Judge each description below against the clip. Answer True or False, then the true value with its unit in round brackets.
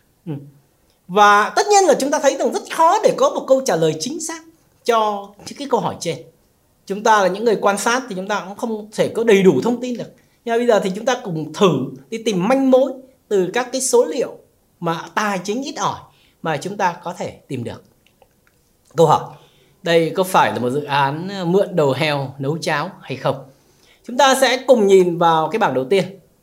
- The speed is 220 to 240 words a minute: True (225 wpm)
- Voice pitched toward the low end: False (205 Hz)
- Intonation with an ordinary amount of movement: False (7.8 semitones)